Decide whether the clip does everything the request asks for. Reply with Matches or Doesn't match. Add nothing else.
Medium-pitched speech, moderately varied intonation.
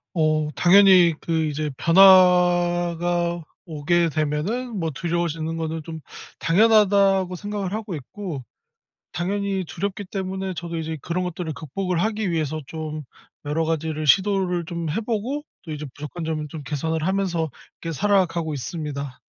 Matches